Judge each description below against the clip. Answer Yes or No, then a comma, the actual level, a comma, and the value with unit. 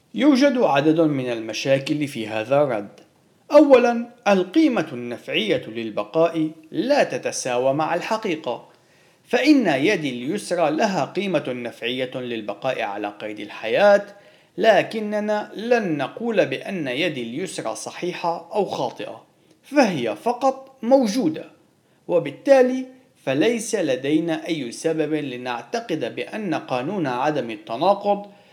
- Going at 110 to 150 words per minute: No, average, 100 wpm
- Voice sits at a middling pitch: Yes, medium, 175 Hz